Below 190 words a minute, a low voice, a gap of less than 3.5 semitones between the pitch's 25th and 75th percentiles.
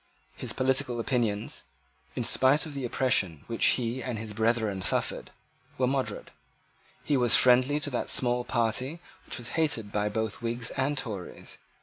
Yes: average, 160 wpm; low, 120 Hz; average, 2.9 semitones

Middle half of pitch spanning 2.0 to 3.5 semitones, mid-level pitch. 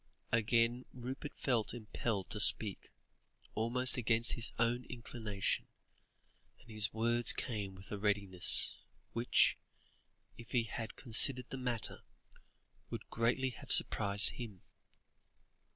No: narrow, 2.4 semitones; low, 115 Hz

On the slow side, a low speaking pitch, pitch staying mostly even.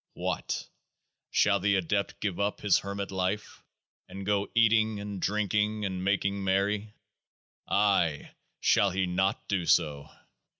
Yes: slow, 130 wpm; low, 100 Hz; narrow, 1.6 semitones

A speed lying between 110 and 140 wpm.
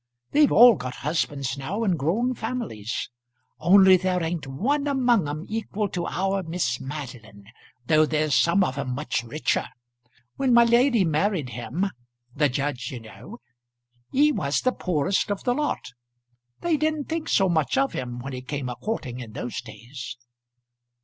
No: average, 165 wpm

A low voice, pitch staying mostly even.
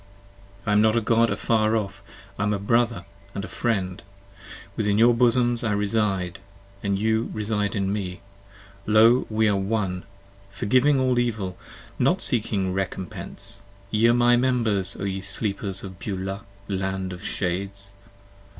No: low, 105 Hz; average, 3.0 semitones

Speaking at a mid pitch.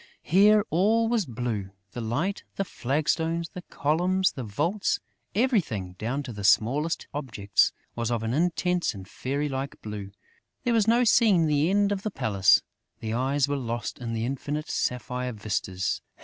Yes: medium, 145 Hz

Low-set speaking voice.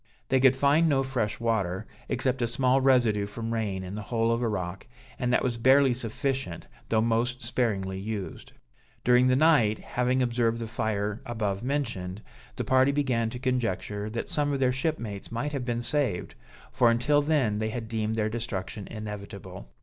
Yes: low, 115 Hz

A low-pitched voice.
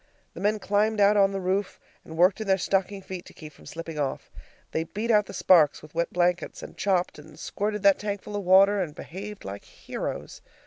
No: high, 190 Hz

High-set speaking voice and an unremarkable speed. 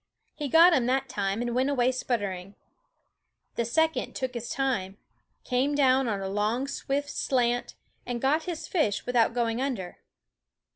Yes: very high, 250 Hz; average, 160 wpm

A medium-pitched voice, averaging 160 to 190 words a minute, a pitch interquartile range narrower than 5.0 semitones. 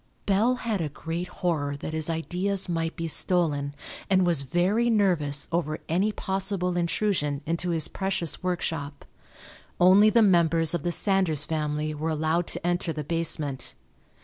No: medium, 170 Hz; average, 150 wpm; average, 3.4 semitones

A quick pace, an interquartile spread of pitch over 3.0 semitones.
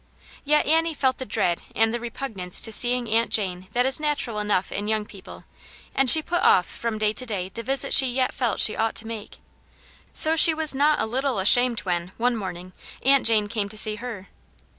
Yes: fast, 210 wpm; average, 4.2 semitones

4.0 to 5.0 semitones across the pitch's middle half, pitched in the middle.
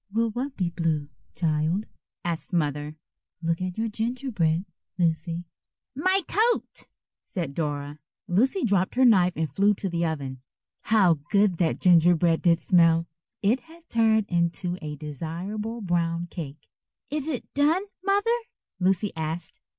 No: wide, 5.4 semitones; medium, 180 Hz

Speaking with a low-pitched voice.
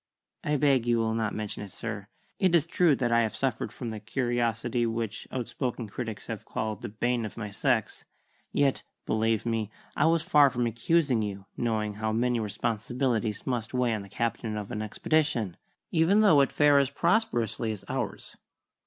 Yes: low, 115 Hz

